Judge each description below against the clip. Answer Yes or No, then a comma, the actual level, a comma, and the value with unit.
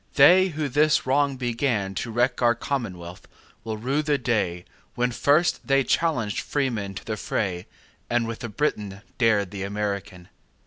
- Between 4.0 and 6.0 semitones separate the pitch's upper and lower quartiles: Yes, wide, 5.4 semitones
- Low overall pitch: Yes, low, 120 Hz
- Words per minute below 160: Yes, average, 140 wpm